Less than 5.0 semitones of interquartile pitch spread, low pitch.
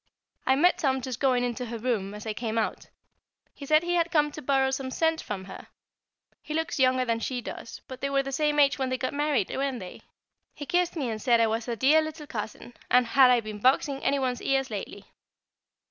No: average, 3.6 semitones; very high, 260 Hz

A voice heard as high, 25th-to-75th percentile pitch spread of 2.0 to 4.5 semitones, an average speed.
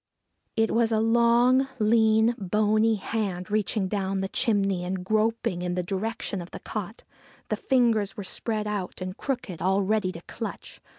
Yes: high, 215 Hz; average, 2.9 semitones; average, 165 wpm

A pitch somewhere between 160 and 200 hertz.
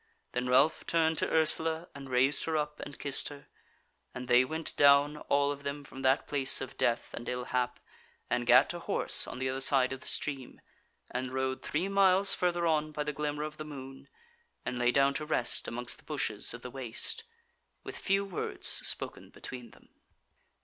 No: medium, 140 Hz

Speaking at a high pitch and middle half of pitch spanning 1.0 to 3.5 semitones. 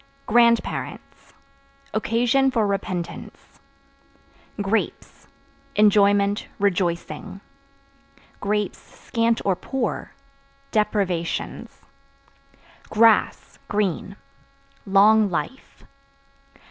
Yes: high, 210 Hz; narrow, 2.6 semitones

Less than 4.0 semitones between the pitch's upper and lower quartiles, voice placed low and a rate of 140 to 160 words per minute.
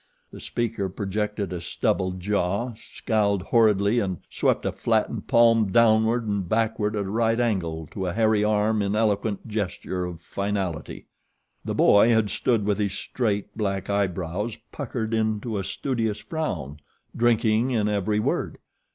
Yes: narrow, 2.5 semitones; low, 105 Hz; average, 150 wpm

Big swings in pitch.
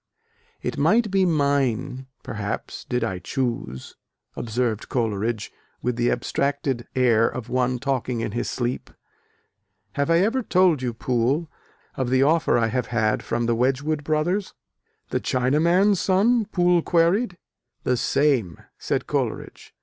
Yes: wide, 5.8 semitones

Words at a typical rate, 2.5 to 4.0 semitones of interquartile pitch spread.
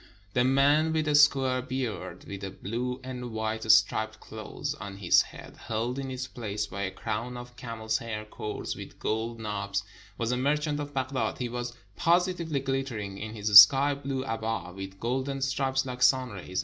Yes: average, 180 wpm; average, 3.7 semitones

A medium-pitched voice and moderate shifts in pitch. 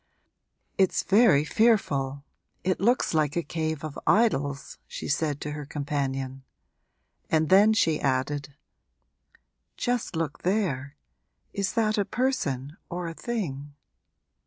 No: medium, 155 Hz; wide, 5.9 semitones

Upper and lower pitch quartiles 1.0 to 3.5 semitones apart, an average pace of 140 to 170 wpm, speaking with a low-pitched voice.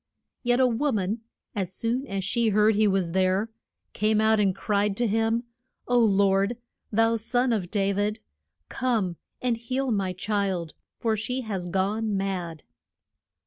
No: average, 2.9 semitones; average, 155 wpm; high, 210 Hz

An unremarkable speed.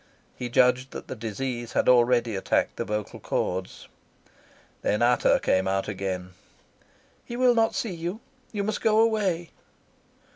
Yes: average, 145 wpm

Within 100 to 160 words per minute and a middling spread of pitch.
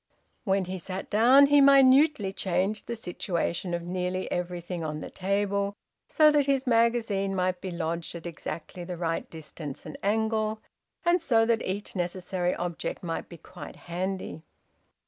Yes: average, 155 wpm; average, 4.2 semitones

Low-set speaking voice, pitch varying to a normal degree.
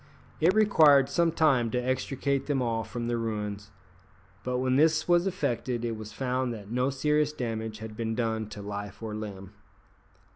Yes: low, 120 Hz; average, 4.2 semitones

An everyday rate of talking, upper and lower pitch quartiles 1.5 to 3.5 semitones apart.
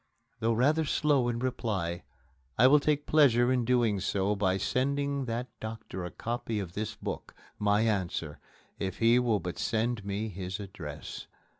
No: average, 160 wpm; average, 4.3 semitones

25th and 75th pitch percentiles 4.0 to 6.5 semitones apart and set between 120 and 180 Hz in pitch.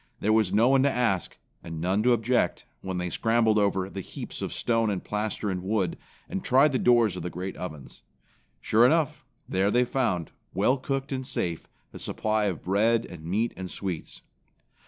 No: average, 4.6 semitones; low, 105 Hz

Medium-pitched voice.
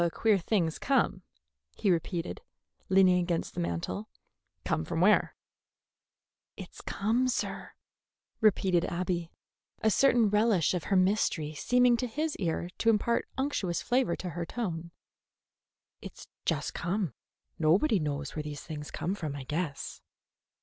Yes: medium, 180 Hz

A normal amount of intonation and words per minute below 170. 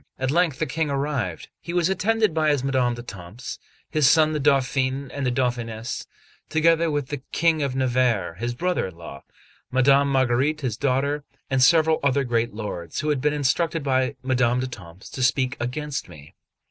No: average, 3.6 semitones; average, 175 wpm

